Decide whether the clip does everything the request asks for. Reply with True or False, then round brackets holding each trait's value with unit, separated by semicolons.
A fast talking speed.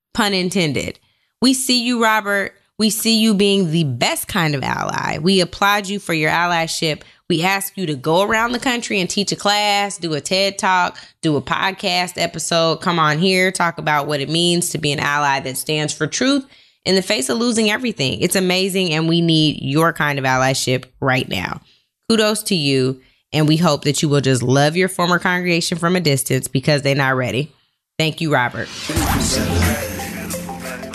False (190 wpm)